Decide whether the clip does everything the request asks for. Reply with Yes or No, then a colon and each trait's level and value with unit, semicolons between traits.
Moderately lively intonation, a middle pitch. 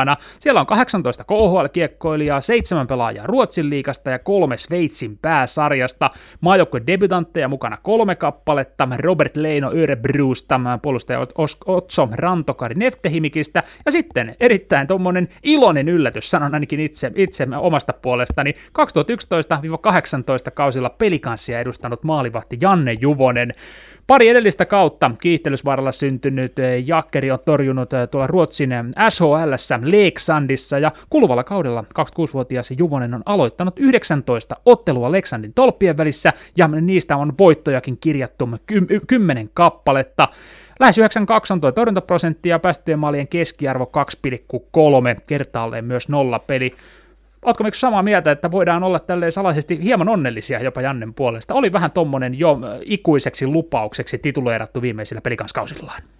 No: wide, 5.7 semitones; medium, 150 Hz